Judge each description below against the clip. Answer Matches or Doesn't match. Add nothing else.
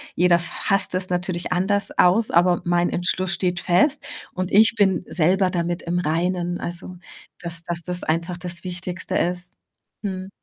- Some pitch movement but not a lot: Doesn't match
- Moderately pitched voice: Matches